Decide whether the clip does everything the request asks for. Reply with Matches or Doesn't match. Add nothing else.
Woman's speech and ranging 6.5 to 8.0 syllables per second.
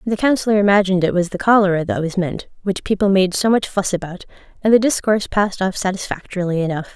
Matches